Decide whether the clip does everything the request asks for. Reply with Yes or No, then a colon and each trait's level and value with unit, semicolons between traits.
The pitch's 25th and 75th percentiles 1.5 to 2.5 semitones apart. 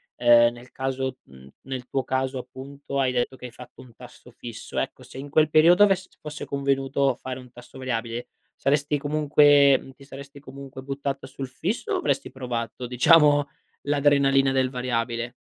Yes: narrow, 2.1 semitones